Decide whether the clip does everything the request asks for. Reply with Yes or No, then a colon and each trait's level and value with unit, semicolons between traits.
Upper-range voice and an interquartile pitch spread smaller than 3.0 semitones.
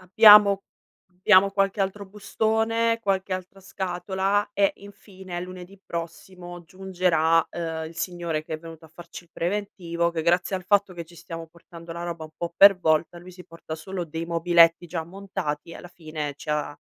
No: medium, 175 Hz; narrow, 2.6 semitones